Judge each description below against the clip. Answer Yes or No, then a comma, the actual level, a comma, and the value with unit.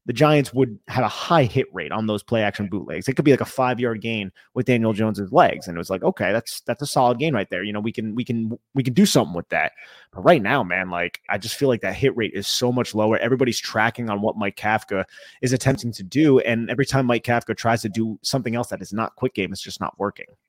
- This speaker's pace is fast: Yes, fast, 275 wpm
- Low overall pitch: Yes, low, 115 Hz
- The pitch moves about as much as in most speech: Yes, average, 3.5 semitones